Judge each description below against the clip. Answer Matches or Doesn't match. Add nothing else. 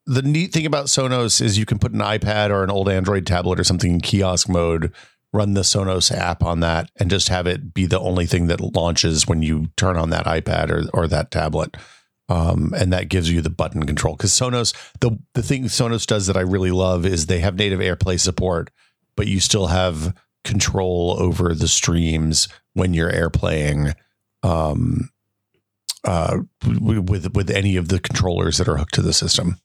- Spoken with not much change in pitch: Doesn't match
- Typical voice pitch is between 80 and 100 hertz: Matches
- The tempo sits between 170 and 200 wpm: Matches